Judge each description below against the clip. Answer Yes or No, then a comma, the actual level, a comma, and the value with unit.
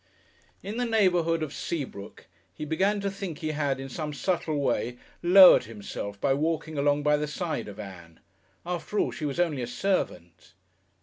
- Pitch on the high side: No, medium, 150 Hz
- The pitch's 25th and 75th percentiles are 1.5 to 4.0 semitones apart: No, average, 5.0 semitones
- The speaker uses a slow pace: No, average, 175 wpm